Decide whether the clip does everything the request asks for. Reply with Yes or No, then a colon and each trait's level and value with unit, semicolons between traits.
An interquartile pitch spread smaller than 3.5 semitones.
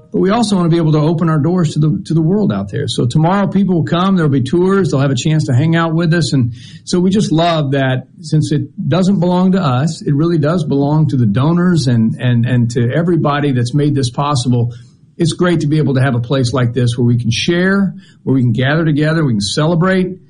No: average, 4.3 semitones